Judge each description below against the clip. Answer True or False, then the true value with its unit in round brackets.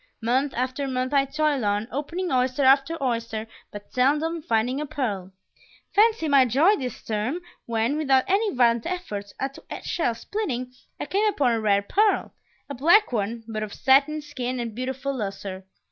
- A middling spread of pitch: True (4.6 semitones)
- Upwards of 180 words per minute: False (165 wpm)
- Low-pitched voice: False (260 Hz)